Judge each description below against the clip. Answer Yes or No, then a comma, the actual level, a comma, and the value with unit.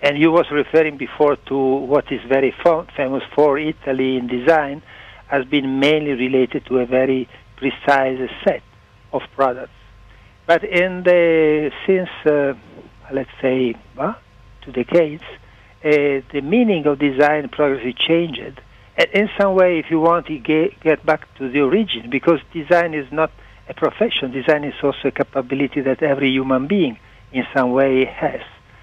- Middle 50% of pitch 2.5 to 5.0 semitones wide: Yes, average, 3.4 semitones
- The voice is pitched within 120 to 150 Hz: Yes, medium, 140 Hz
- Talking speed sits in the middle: Yes, average, 160 wpm